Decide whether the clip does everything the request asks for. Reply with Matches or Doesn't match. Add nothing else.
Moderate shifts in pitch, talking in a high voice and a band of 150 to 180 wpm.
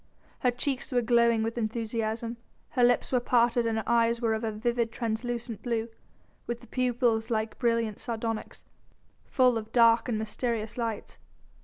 Doesn't match